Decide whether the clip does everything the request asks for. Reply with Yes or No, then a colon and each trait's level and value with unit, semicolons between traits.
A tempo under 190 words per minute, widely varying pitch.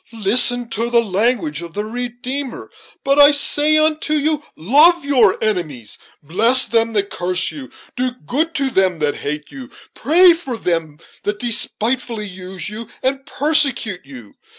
Yes: average, 150 wpm; wide, 6.7 semitones